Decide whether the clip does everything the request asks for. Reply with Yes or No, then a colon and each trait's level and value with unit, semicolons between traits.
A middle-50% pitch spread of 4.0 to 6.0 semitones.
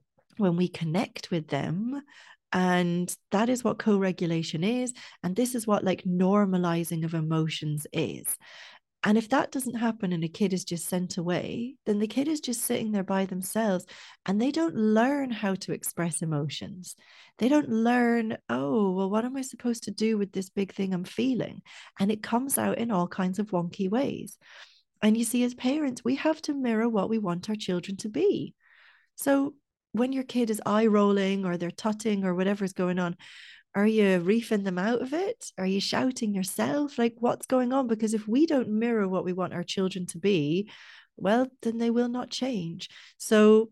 Yes: average, 4.7 semitones